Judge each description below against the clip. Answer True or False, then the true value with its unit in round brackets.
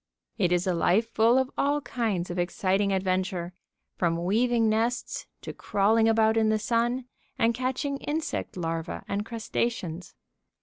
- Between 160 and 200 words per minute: False (145 wpm)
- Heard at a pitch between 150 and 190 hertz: False (220 Hz)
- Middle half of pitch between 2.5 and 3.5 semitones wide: False (4.3 semitones)